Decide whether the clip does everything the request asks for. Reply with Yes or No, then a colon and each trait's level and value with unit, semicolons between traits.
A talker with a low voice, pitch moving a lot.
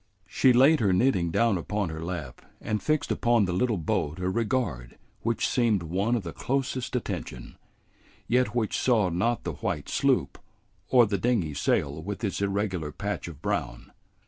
Yes: low, 100 Hz; wide, 5.9 semitones